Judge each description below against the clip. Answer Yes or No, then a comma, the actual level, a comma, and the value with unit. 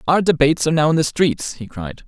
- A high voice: No, medium, 145 Hz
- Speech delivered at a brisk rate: Yes, fast, 260 wpm